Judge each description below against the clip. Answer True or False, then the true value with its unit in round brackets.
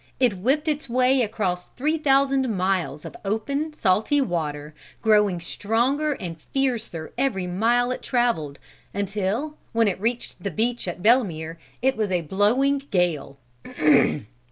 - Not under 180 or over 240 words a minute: False (135 wpm)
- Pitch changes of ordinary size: False (6.6 semitones)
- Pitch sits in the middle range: False (220 Hz)